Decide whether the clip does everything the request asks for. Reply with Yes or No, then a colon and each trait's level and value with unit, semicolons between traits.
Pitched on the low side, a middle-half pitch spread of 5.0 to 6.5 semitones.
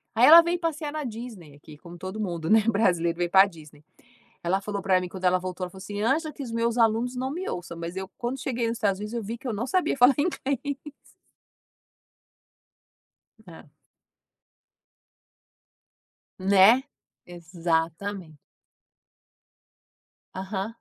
No: high, 205 Hz; wide, 5.6 semitones